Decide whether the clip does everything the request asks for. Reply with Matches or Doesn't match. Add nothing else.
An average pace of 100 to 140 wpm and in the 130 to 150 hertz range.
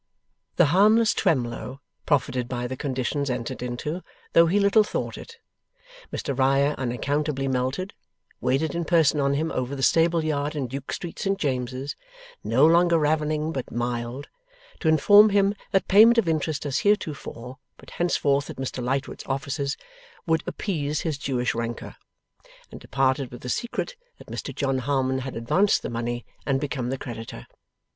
Doesn't match